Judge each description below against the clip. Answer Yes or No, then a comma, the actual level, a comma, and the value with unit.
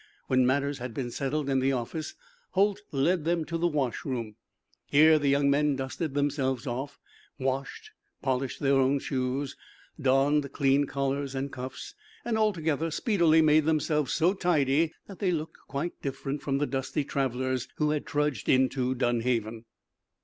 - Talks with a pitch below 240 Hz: Yes, medium, 140 Hz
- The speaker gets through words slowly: No, average, 155 wpm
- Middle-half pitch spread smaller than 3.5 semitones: Yes, average, 2.8 semitones